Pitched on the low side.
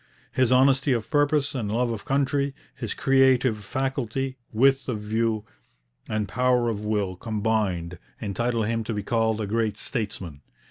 Yes: low, 115 Hz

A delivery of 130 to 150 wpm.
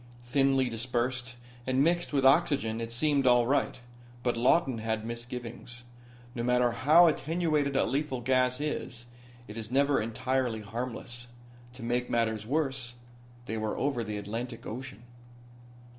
Yes: average, 140 wpm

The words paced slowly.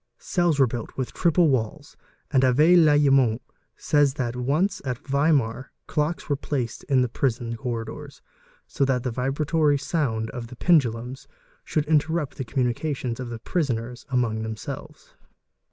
No: average, 150 wpm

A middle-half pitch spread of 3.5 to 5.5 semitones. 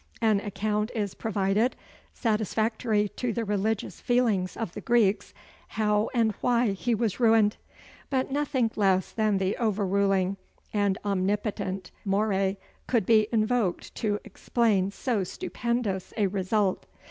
No: narrow, 2.5 semitones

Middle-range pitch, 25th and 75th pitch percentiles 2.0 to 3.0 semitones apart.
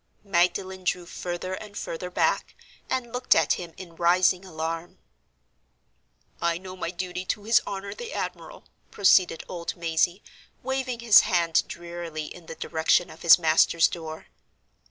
Yes: medium, 180 Hz; narrow, 2.4 semitones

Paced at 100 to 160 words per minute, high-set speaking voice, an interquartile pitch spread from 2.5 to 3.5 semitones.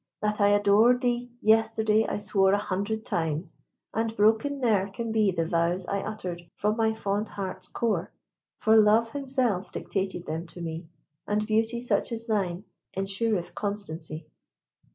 Yes: average, 155 wpm; high, 210 Hz; average, 3.0 semitones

